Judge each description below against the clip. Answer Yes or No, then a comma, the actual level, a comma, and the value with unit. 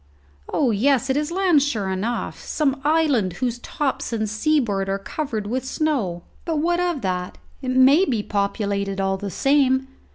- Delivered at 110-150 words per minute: No, average, 165 wpm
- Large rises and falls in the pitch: Yes, wide, 6.6 semitones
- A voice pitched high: Yes, very high, 255 Hz